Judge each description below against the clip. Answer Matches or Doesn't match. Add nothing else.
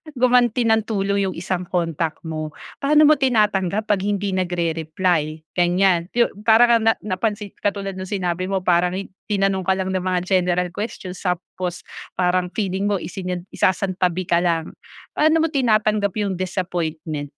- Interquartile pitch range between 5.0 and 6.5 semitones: Doesn't match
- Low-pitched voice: Doesn't match